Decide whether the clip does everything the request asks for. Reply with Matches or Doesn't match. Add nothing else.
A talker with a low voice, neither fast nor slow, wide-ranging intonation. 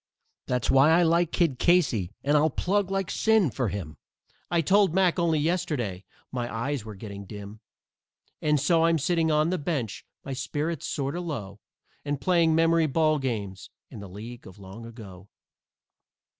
Doesn't match